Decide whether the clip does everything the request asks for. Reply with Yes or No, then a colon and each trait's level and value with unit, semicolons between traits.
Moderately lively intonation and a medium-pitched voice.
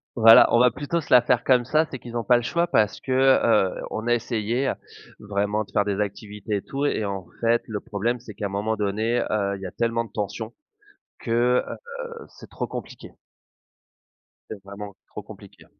No: average, 3.0 semitones; low, 110 Hz